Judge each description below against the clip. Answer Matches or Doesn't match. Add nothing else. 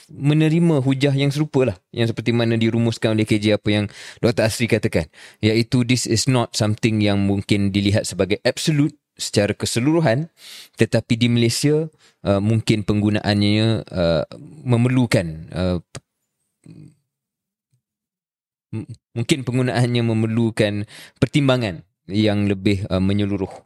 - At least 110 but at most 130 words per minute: Matches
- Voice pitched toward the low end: Matches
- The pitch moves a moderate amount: Matches